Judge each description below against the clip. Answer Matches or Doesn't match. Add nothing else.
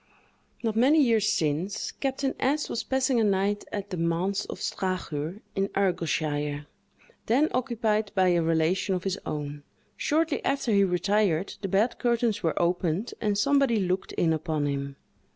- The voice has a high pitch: Matches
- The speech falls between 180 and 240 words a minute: Doesn't match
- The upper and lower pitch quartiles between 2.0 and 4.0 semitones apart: Doesn't match